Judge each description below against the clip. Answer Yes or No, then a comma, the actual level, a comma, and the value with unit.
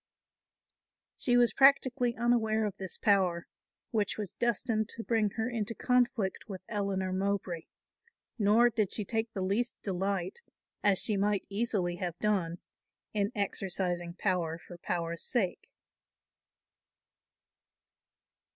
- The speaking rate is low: Yes, slow, 120 wpm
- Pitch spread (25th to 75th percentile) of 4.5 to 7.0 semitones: No, average, 3.4 semitones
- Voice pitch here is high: Yes, high, 205 Hz